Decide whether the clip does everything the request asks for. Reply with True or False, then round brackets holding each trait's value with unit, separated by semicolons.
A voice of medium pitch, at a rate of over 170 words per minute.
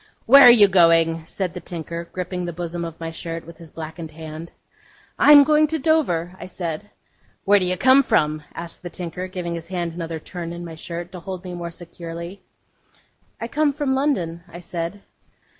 True (175 Hz; 195 wpm)